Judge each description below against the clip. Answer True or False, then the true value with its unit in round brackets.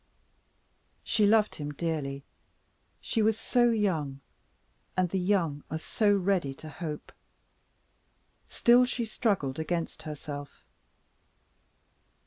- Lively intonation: True (6.2 semitones)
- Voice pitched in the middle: True (170 Hz)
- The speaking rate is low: True (105 wpm)